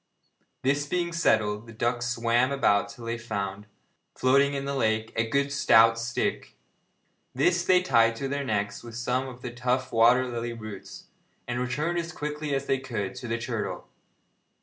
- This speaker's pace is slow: No, average, 170 wpm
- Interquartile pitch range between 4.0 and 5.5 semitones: No, average, 3.4 semitones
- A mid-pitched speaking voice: No, low, 120 Hz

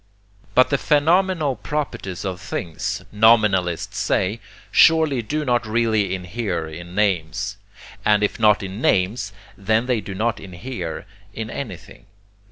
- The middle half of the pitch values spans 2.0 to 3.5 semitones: No, average, 4.3 semitones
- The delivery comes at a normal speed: No, slow, 130 wpm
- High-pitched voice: No, low, 105 Hz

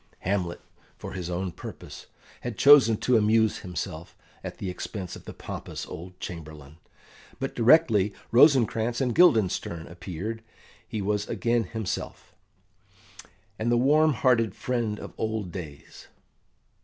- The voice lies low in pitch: Yes, low, 110 Hz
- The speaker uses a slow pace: Yes, slow, 130 wpm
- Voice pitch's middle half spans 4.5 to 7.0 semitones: Yes, average, 4.8 semitones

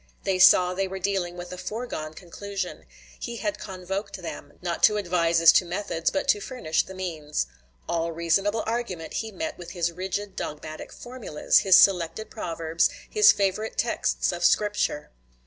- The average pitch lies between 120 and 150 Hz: No, medium, 185 Hz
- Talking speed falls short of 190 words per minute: Yes, average, 165 wpm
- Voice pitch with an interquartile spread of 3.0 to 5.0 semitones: Yes, average, 3.5 semitones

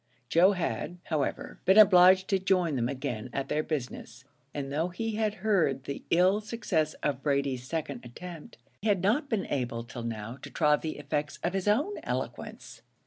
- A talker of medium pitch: Yes, medium, 160 Hz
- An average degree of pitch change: No, wide, 5.9 semitones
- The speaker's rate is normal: Yes, average, 180 wpm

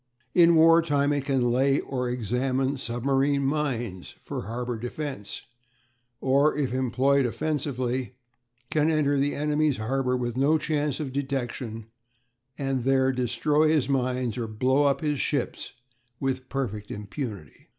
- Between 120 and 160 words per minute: Yes, slow, 135 wpm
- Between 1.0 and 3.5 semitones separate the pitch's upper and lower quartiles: Yes, average, 2.8 semitones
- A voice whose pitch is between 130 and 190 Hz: Yes, low, 135 Hz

